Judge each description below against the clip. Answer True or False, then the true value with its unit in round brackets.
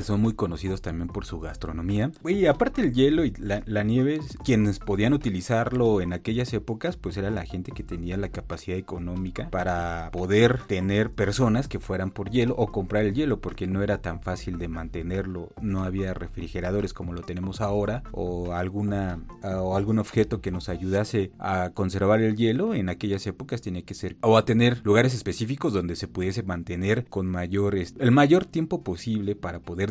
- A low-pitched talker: True (100 Hz)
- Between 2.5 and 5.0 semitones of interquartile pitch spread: True (3.6 semitones)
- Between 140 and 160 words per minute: False (185 wpm)